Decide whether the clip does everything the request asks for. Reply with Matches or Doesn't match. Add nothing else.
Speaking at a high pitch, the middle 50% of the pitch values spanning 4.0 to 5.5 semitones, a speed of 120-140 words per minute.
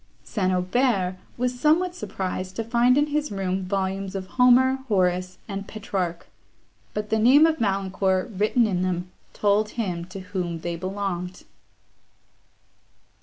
Matches